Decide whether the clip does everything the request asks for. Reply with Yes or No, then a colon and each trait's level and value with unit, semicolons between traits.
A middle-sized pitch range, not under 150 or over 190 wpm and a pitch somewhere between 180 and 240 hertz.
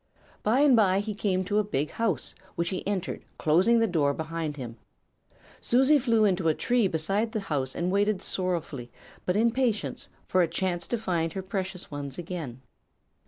Yes: average, 4.8 semitones; average, 180 wpm; medium, 185 Hz